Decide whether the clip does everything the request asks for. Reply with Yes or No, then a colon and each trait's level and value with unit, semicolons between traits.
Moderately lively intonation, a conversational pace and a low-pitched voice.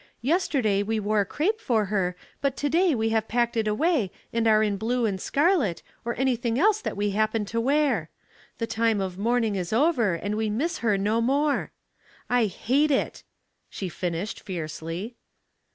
No: average, 4.6 semitones; average, 175 wpm; high, 225 Hz